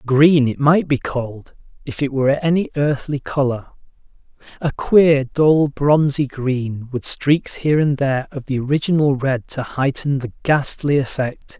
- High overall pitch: No, medium, 140 Hz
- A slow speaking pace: No, average, 150 wpm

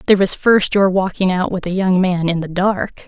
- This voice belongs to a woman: Yes, female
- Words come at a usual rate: No, fast, 255 wpm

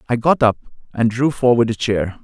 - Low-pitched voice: Yes, low, 115 Hz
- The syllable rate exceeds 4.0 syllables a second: Yes, 5.4 syllables/s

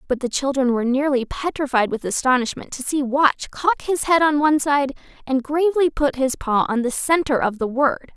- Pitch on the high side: Yes, very high, 275 Hz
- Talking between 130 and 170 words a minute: No, fast, 205 wpm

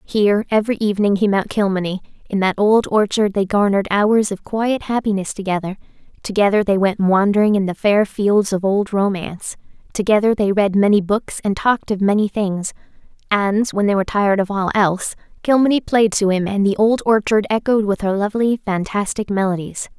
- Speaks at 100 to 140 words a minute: No, average, 180 wpm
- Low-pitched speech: No, high, 205 Hz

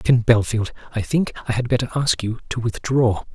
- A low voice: Yes, low, 120 Hz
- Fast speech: No, average, 195 wpm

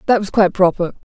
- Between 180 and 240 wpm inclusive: Yes, fast, 205 wpm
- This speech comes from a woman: Yes, female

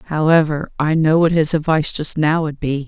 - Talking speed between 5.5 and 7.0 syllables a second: No, 5.1 syllables/s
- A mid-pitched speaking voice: Yes, medium, 155 Hz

